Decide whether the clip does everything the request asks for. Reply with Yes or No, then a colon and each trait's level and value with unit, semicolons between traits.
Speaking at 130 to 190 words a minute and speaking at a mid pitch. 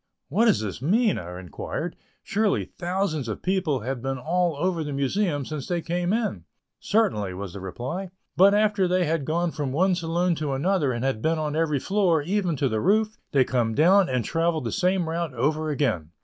No: average, 200 wpm; medium, 160 Hz